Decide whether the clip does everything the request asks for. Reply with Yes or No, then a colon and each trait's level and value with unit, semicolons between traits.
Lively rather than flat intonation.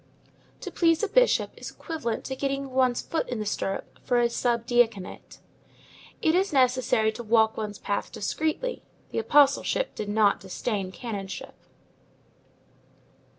No: average, 4.4 semitones